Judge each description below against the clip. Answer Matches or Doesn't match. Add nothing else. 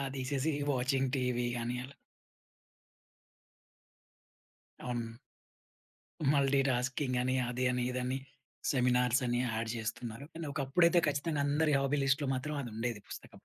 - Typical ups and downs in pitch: Doesn't match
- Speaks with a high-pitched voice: Doesn't match